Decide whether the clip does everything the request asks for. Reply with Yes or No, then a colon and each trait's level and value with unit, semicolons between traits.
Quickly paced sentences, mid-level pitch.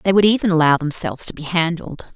Yes: fast, 225 wpm; medium, 170 Hz